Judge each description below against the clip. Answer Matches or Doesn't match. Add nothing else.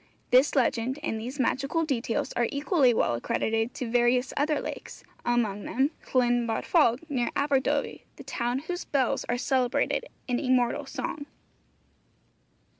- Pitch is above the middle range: Matches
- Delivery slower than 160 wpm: Matches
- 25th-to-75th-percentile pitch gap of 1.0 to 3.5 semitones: Matches